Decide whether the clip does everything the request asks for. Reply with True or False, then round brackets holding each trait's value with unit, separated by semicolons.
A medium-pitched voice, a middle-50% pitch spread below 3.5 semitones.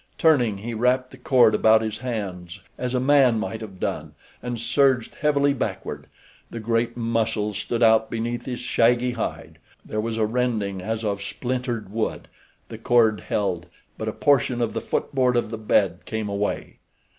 False (115 Hz; 2.5 semitones)